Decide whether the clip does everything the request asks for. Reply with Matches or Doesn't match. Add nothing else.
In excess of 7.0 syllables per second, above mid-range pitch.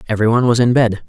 Doesn't match